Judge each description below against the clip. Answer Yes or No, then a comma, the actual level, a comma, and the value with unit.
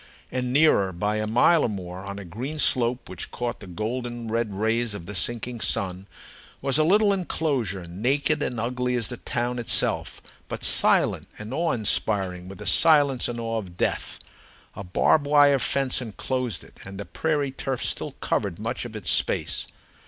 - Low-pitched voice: Yes, low, 120 Hz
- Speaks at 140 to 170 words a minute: No, average, 180 wpm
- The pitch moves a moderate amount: Yes, average, 4.6 semitones